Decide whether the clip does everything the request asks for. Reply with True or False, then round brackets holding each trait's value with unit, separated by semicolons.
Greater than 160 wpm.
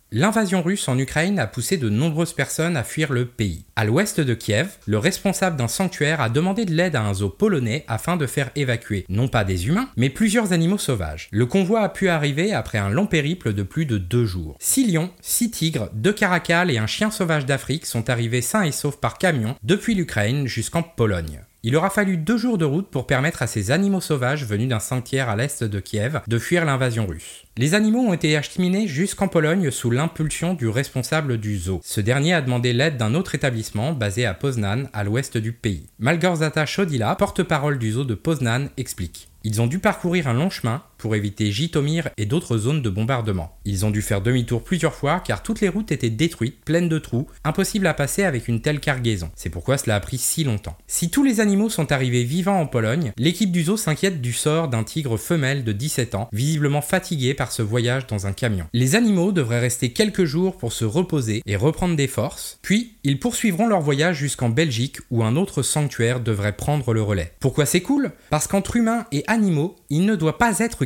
True (215 wpm)